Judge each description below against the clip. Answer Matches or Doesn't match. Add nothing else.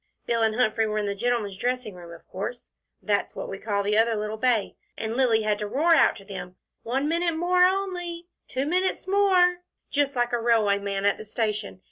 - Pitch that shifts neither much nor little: Doesn't match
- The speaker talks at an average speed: Doesn't match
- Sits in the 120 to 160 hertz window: Doesn't match